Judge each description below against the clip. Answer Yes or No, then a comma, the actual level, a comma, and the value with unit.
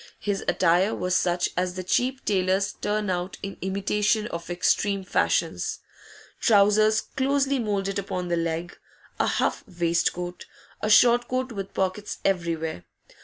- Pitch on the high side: Yes, high, 195 Hz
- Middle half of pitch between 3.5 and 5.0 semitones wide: No, average, 3.0 semitones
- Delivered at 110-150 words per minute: Yes, slow, 135 wpm